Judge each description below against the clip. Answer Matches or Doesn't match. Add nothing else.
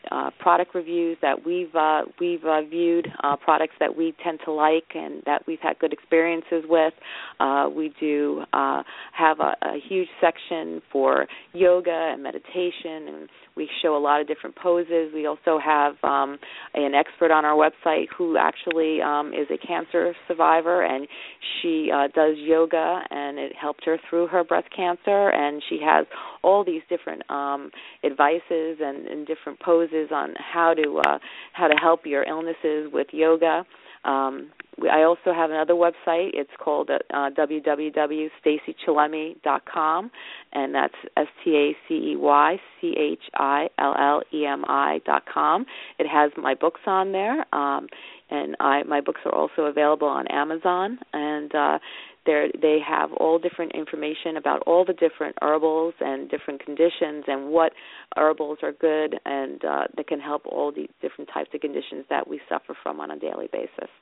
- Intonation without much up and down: Matches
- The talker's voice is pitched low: Doesn't match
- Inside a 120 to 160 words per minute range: Matches